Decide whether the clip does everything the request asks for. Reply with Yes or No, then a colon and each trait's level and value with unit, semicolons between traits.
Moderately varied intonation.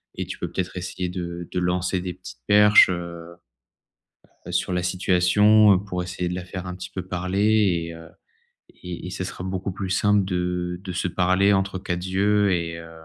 No: narrow, 1.3 semitones